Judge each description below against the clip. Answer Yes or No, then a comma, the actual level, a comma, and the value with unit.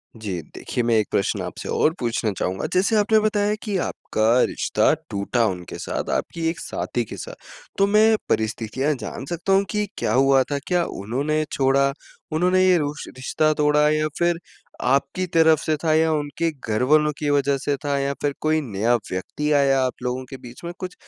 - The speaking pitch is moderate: Yes, medium, 145 Hz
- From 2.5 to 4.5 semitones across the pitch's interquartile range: No, average, 5.0 semitones